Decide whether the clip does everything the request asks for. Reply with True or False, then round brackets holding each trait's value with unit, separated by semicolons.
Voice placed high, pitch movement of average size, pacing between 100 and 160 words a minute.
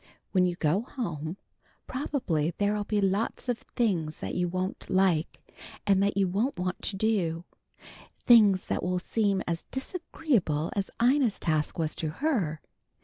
True (195 Hz; 4.9 semitones; 150 wpm)